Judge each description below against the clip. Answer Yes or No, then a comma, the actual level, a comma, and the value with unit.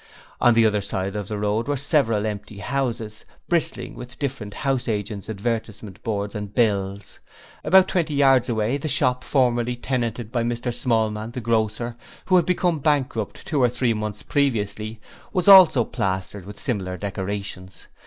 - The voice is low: Yes, low, 115 Hz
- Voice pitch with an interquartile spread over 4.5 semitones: No, average, 3.9 semitones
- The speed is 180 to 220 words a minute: No, average, 160 wpm